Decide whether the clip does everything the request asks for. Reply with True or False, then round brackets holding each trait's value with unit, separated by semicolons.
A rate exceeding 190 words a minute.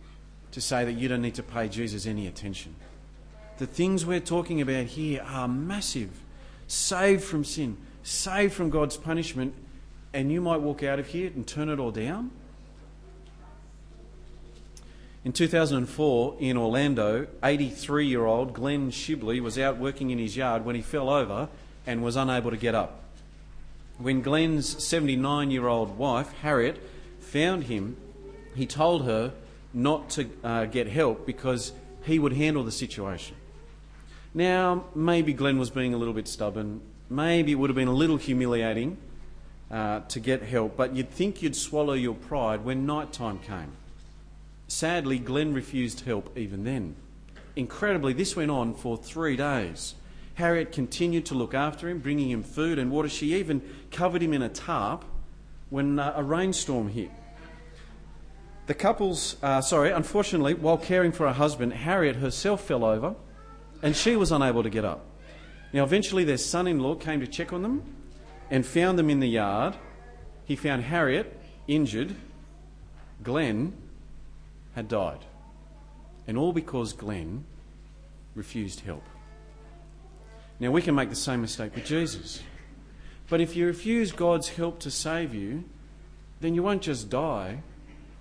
False (155 wpm)